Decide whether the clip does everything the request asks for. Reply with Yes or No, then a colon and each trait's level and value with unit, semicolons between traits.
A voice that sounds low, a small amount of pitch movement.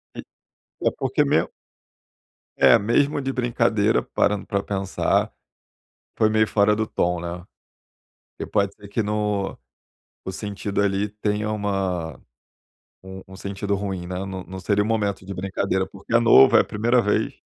Yes: low, 100 Hz; narrow, 1.9 semitones